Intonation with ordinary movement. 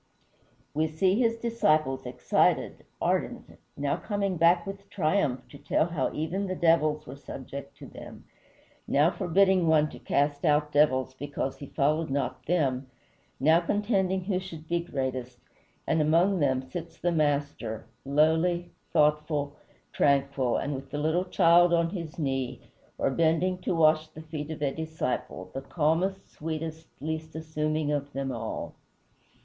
Yes: average, 3.5 semitones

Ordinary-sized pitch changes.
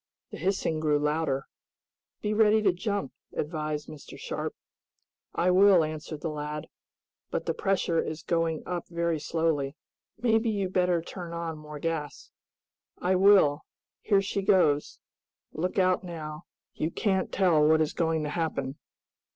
Yes: average, 3.7 semitones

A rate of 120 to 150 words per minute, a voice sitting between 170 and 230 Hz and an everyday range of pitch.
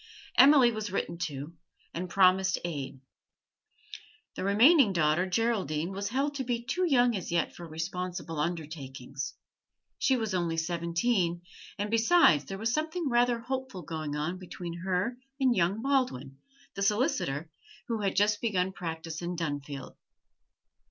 No: average, 140 wpm; medium, 185 Hz; wide, 6.3 semitones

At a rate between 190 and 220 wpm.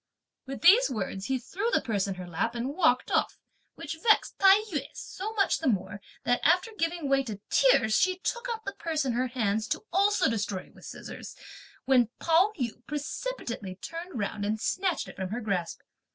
Yes: average, 200 wpm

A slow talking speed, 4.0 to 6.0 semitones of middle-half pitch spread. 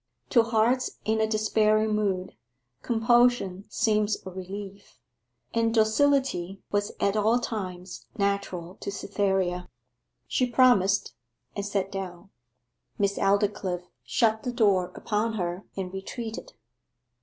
No: slow, 115 wpm; narrow, 2.6 semitones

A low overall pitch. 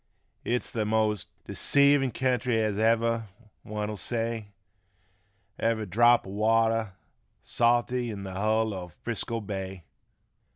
Yes: low, 110 Hz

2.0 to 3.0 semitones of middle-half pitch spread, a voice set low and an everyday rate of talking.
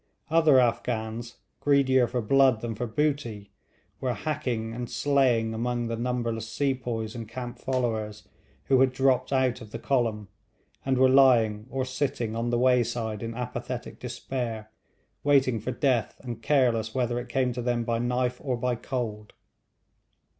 Yes: narrow, 2.4 semitones; low, 120 Hz; average, 155 wpm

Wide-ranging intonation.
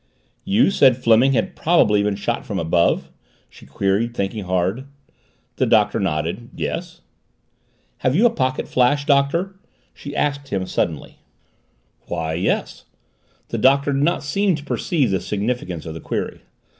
Yes: wide, 7.0 semitones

